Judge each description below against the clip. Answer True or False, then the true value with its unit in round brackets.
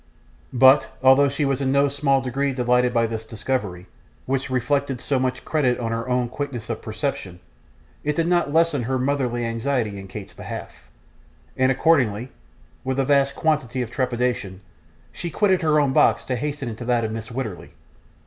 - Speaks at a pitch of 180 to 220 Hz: False (130 Hz)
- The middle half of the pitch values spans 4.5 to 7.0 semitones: False (3.2 semitones)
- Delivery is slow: False (175 wpm)